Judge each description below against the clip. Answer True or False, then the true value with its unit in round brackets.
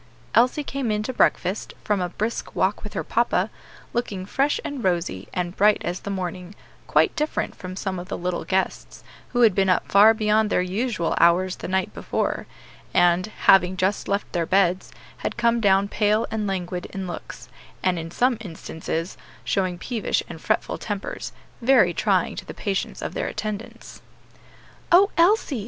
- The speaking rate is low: False (175 wpm)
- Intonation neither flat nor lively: True (3.5 semitones)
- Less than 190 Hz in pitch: False (195 Hz)